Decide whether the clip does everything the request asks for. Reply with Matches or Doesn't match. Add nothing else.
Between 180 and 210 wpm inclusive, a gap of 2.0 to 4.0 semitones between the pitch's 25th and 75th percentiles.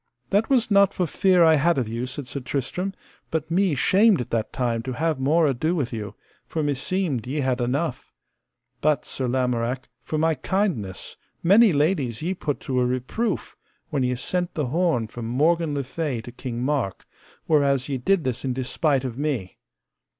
Doesn't match